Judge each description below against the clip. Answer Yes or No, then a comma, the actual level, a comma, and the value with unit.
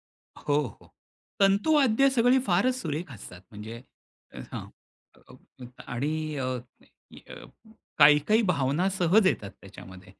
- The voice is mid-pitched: Yes, medium, 155 Hz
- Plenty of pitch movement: Yes, wide, 8.4 semitones